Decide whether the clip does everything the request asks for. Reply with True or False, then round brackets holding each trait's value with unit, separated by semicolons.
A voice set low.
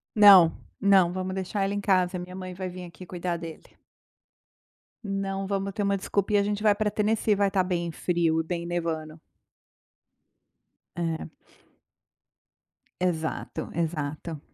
False (185 Hz)